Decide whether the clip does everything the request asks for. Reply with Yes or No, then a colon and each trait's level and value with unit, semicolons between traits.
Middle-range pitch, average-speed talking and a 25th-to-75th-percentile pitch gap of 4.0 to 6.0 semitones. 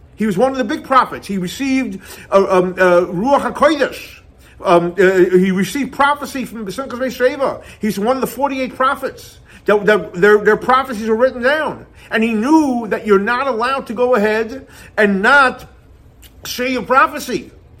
No: high, 235 Hz; average, 160 wpm; average, 4.3 semitones